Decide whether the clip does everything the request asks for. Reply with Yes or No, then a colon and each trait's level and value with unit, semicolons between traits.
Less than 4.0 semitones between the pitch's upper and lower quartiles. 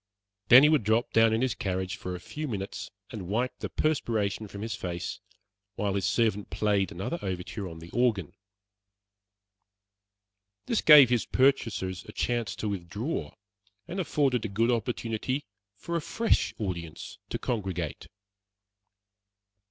No: average, 4.6 semitones